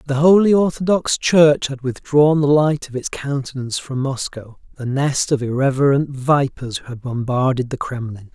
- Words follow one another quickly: No, average, 165 wpm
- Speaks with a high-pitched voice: No, low, 135 Hz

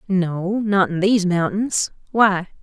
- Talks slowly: Yes, slow, 90 wpm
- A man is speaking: No, female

